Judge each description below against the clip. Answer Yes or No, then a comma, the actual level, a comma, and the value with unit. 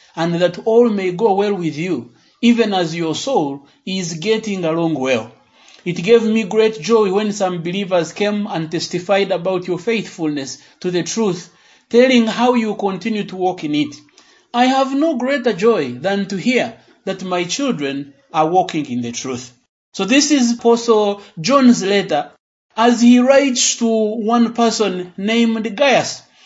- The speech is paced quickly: No, average, 160 wpm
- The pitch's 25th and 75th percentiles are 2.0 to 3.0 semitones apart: No, average, 5.0 semitones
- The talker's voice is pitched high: Yes, high, 200 Hz